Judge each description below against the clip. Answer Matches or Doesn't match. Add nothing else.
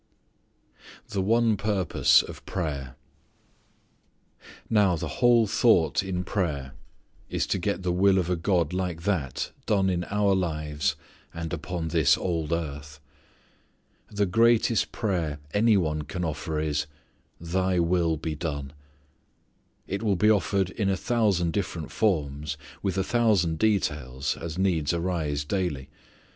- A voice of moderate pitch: Doesn't match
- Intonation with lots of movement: Doesn't match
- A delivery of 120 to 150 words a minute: Matches